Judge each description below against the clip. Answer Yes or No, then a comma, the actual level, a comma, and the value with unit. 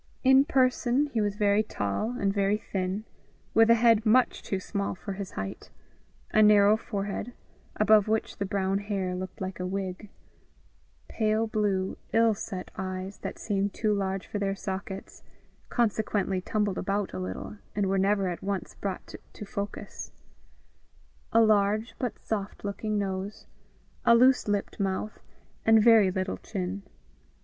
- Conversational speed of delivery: Yes, average, 150 wpm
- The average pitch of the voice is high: Yes, high, 200 Hz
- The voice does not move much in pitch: Yes, narrow, 2.1 semitones